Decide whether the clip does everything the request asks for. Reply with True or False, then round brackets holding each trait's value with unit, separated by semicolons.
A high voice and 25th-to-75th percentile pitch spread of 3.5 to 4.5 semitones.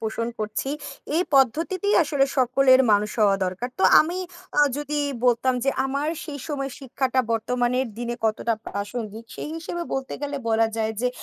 True (255 Hz; 4.0 semitones)